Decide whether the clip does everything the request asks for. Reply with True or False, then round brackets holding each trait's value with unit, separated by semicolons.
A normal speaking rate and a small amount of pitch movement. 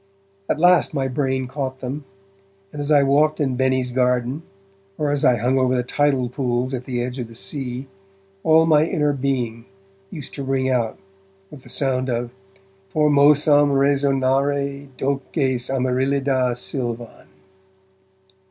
True (145 wpm; 2.2 semitones)